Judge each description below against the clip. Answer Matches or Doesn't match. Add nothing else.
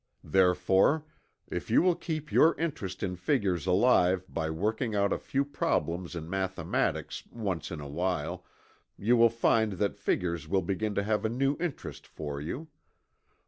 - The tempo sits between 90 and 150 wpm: Doesn't match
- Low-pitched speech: Matches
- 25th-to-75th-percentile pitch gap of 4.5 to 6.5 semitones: Matches